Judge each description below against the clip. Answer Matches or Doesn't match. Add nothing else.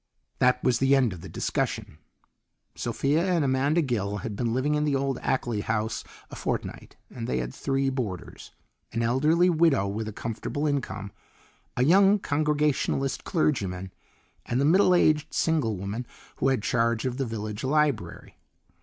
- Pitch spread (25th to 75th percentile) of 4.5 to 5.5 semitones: Matches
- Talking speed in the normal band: Matches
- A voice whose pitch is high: Doesn't match